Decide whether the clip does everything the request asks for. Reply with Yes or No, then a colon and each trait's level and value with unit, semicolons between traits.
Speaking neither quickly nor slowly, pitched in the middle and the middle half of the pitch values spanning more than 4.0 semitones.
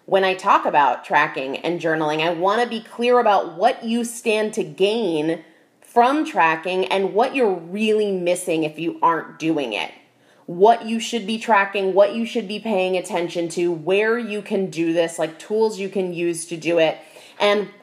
No: average, 190 wpm; high, 195 Hz; average, 4.5 semitones